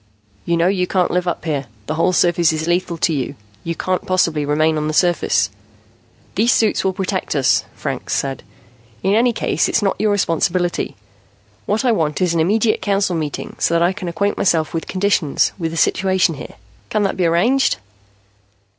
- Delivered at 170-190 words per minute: Yes, average, 185 wpm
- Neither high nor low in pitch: Yes, medium, 175 Hz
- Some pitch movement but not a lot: Yes, average, 3.4 semitones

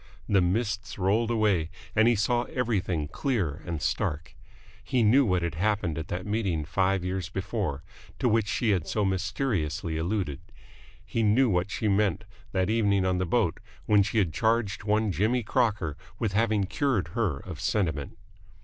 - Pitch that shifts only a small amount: No, average, 3.9 semitones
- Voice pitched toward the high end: No, low, 100 Hz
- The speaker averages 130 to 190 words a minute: Yes, average, 170 wpm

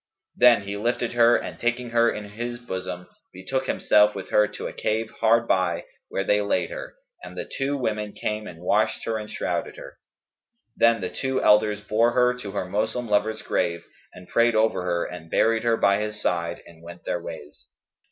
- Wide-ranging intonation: No, average, 4.0 semitones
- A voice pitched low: Yes, low, 105 Hz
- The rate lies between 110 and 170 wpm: No, average, 195 wpm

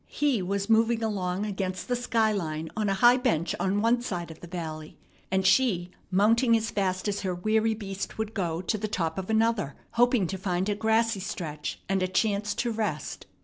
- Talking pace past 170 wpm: Yes, average, 200 wpm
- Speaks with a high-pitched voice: Yes, high, 200 Hz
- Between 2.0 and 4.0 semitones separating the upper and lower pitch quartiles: Yes, average, 3.5 semitones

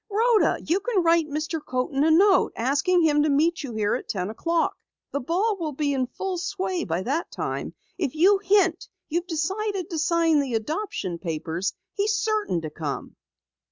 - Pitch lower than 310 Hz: No, very high, 320 Hz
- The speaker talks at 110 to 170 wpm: No, average, 180 wpm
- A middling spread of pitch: No, wide, 6.2 semitones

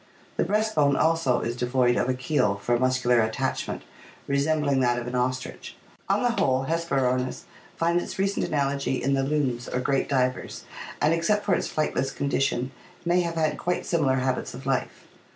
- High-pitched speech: No, low, 135 Hz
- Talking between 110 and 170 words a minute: No, average, 185 wpm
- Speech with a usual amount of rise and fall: Yes, average, 4.1 semitones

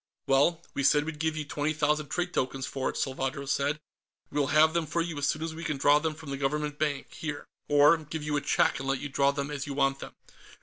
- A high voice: No, medium, 145 Hz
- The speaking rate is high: Yes, fast, 255 wpm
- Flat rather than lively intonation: Yes, narrow, 2.0 semitones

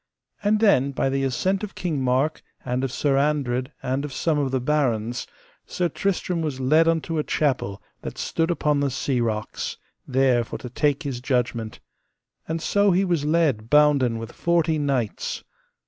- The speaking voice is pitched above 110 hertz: Yes, medium, 140 Hz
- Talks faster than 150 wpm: Yes, average, 175 wpm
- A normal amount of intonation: Yes, average, 4.2 semitones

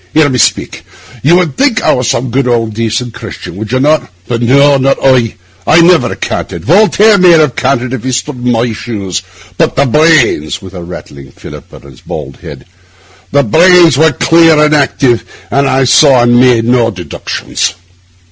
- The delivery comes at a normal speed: Yes, average, 180 wpm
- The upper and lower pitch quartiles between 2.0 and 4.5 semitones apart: No, average, 4.9 semitones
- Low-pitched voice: Yes, low, 130 Hz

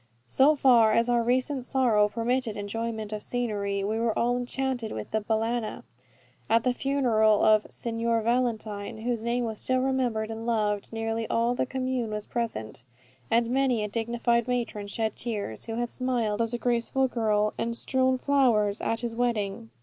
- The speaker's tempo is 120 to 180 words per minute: Yes, average, 170 wpm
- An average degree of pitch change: No, narrow, 2.2 semitones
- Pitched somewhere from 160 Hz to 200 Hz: No, high, 230 Hz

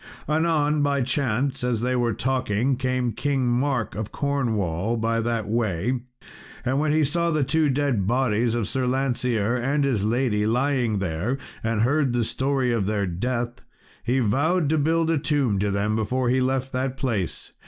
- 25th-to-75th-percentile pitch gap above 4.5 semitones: No, average, 3.8 semitones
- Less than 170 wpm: No, average, 175 wpm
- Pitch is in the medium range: No, low, 125 Hz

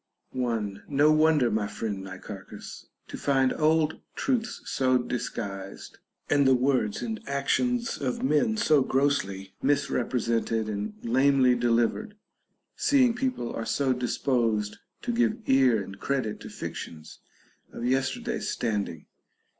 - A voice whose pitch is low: Yes, low, 130 Hz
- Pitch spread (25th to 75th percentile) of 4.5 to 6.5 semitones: Yes, average, 5.1 semitones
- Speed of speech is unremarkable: No, slow, 120 wpm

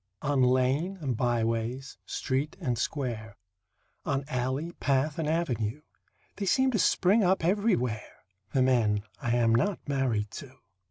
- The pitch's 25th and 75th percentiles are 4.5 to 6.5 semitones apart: Yes, average, 4.8 semitones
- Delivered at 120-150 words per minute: Yes, average, 140 wpm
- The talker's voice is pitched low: Yes, low, 130 Hz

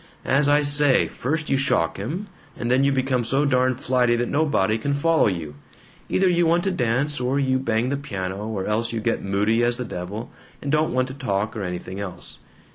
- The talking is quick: Yes, fast, 210 wpm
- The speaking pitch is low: Yes, low, 125 Hz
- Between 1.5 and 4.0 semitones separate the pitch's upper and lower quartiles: No, average, 4.8 semitones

